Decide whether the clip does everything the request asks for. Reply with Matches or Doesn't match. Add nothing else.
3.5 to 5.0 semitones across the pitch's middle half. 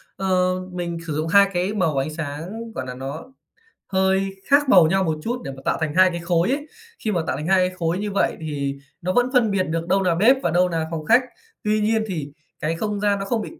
Matches